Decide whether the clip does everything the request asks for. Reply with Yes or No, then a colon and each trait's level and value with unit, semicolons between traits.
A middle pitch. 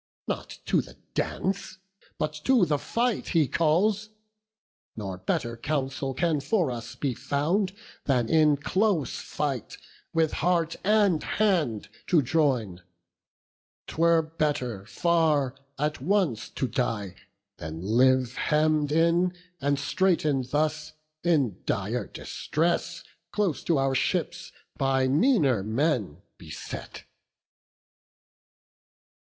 Yes: medium, 150 Hz